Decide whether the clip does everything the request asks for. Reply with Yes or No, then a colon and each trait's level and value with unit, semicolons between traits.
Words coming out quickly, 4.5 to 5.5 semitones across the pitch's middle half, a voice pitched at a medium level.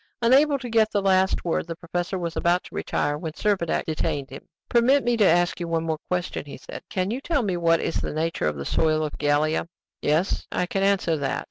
No: fast, 230 wpm; average, 4.1 semitones; medium, 175 Hz